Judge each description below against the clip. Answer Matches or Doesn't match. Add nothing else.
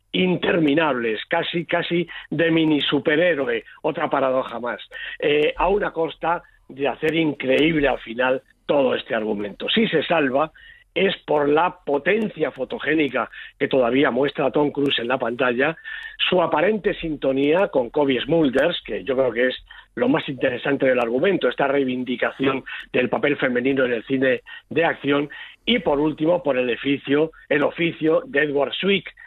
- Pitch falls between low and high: Matches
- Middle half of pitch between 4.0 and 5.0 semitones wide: Matches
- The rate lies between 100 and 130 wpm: Doesn't match